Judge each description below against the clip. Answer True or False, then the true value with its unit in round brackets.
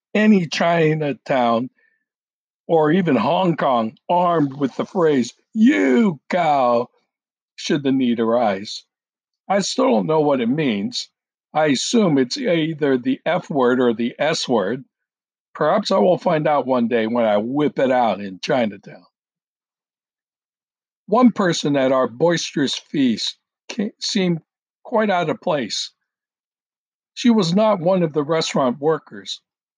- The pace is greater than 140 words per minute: False (135 wpm)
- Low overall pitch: False (170 Hz)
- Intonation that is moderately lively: False (8.1 semitones)